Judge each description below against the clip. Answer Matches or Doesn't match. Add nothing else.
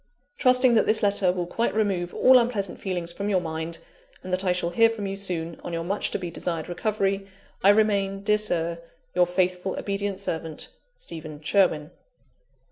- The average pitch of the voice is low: Doesn't match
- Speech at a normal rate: Matches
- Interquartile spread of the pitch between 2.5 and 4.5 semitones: Matches